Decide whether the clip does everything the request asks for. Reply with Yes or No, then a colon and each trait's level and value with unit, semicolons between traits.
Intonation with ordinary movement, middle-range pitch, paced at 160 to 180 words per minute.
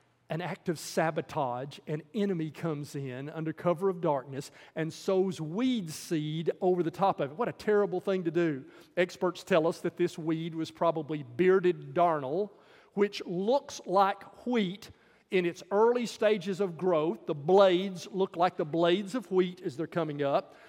Yes: average, 3.4 semitones; medium, 175 Hz; average, 170 wpm